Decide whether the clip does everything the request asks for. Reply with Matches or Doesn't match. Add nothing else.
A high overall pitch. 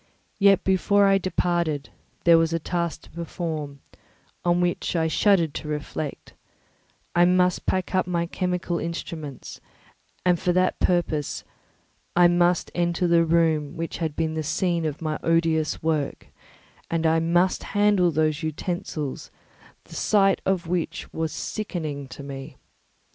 Doesn't match